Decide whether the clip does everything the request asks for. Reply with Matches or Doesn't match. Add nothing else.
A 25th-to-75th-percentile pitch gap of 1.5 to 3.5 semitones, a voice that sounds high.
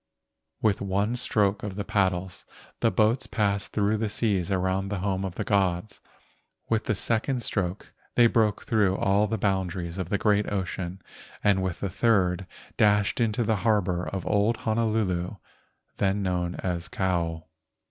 Doesn't match